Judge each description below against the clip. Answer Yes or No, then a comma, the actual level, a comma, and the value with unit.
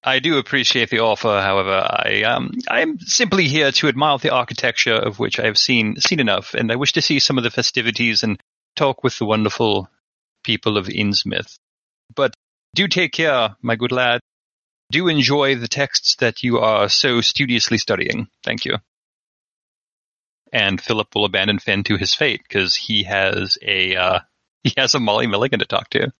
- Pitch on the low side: Yes, low, 125 Hz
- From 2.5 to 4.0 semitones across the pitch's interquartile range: No, average, 4.5 semitones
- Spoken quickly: No, average, 180 wpm